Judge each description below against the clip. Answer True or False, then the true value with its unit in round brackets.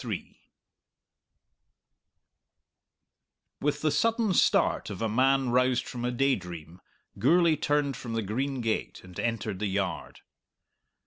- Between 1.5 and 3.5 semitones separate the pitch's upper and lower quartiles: False (4.9 semitones)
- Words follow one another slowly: True (115 wpm)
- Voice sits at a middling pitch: False (125 Hz)